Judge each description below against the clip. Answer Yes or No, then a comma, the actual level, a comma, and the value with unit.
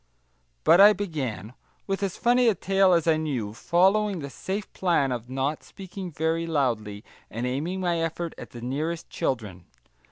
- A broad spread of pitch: Yes, wide, 6.8 semitones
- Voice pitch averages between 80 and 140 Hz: No, medium, 165 Hz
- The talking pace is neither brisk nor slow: Yes, average, 165 wpm